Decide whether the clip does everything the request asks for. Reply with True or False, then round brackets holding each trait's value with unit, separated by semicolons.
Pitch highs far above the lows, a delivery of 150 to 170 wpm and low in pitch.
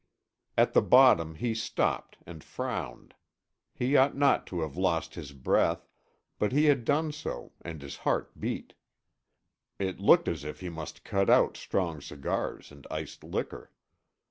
True (8.3 semitones; 155 wpm; 90 Hz)